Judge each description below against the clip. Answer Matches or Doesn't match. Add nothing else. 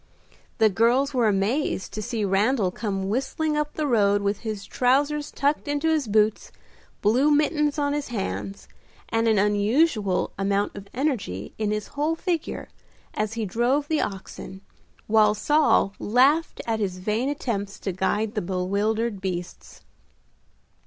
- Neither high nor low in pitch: Doesn't match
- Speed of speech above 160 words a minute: Doesn't match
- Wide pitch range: Matches